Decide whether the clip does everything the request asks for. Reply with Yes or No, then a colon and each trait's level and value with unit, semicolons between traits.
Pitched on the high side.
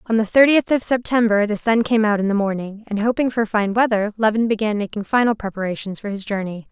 Yes: high, 215 Hz